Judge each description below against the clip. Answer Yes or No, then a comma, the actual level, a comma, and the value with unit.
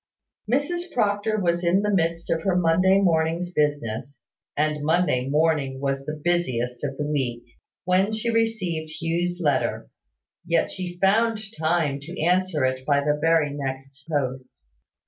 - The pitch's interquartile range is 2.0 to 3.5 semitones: No, average, 4.4 semitones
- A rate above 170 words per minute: No, average, 145 wpm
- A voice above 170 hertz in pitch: No, medium, 165 Hz